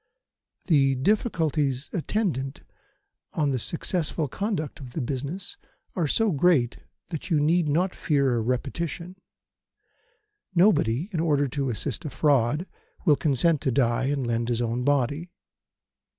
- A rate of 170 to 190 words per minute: No, slow, 135 wpm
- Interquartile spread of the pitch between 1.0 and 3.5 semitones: No, average, 4.5 semitones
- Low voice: No, medium, 145 Hz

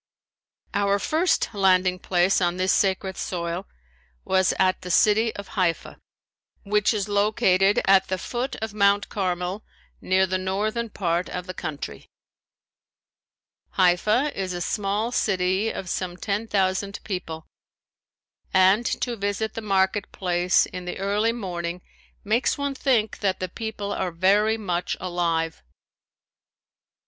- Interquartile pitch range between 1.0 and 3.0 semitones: Yes, narrow, 2.5 semitones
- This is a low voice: No, high, 195 Hz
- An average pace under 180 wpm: Yes, slow, 135 wpm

